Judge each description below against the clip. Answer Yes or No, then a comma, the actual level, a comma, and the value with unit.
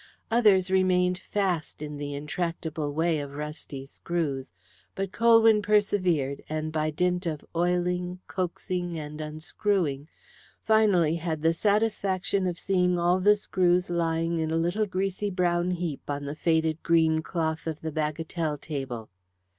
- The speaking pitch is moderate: Yes, medium, 170 Hz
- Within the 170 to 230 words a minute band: No, average, 140 wpm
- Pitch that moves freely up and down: No, average, 3.0 semitones